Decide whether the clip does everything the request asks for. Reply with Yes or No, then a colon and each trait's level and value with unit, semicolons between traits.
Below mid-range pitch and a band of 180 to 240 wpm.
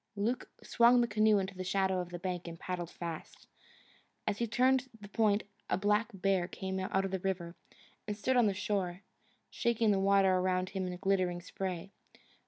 No: high, 195 Hz; average, 190 wpm